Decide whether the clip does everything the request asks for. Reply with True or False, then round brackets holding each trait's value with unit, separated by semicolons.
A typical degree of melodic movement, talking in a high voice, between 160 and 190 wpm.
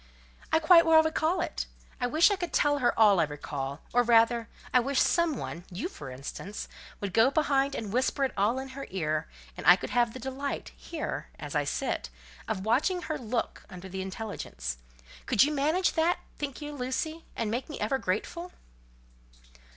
False (7.1 semitones; 255 Hz; 180 wpm)